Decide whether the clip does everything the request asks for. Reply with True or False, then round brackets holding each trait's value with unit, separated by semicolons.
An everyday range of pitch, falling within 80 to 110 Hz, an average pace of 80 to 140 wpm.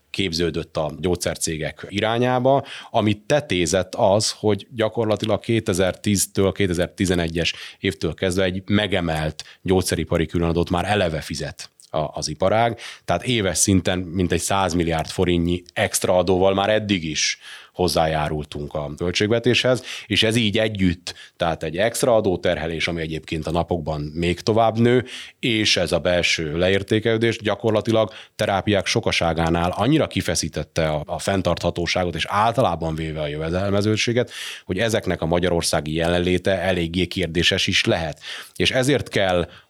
True (3.8 semitones; 95 Hz; 120 wpm)